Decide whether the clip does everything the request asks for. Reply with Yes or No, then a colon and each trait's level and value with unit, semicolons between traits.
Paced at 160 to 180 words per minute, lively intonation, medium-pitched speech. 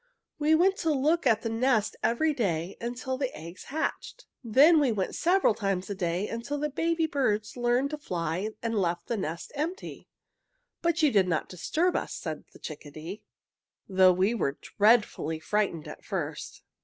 No: average, 170 wpm; wide, 8.0 semitones; high, 230 Hz